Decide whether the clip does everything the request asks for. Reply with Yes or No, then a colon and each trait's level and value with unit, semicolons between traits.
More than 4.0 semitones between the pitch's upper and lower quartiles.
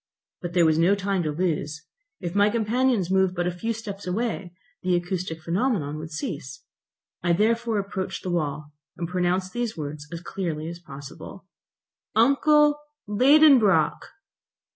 Yes: average, 4.6 semitones